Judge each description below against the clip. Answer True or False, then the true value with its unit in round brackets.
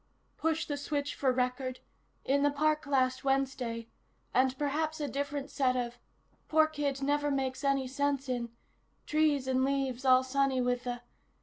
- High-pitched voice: True (275 Hz)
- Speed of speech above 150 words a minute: True (165 wpm)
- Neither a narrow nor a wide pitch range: False (2.0 semitones)